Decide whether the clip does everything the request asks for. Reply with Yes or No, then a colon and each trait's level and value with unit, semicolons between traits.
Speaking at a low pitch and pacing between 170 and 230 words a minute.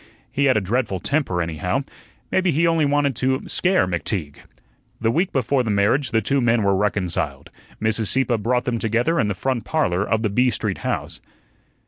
Yes: low, 115 Hz; average, 185 wpm